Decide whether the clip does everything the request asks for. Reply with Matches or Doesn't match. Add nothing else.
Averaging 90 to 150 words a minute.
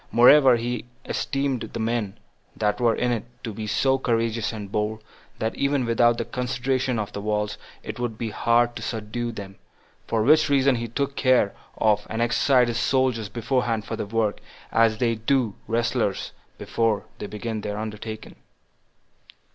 Doesn't match